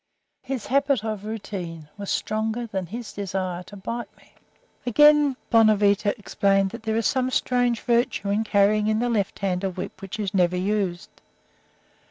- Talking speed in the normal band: Yes, average, 165 wpm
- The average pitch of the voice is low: No, high, 210 Hz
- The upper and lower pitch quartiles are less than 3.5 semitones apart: Yes, average, 3.1 semitones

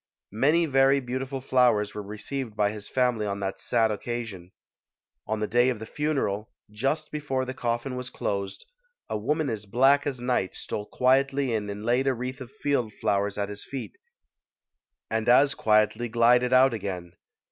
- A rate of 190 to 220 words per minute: No, average, 175 wpm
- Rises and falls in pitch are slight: No, average, 4.1 semitones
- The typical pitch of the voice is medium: No, low, 120 Hz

